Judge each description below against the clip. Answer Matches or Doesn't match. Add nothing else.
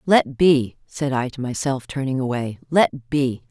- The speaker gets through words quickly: Doesn't match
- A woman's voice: Matches